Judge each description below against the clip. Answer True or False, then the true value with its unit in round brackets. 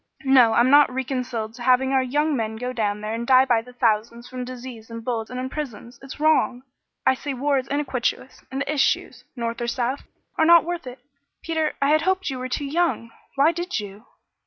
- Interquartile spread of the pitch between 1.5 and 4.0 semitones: True (3.3 semitones)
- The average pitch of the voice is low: False (255 Hz)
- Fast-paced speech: True (215 wpm)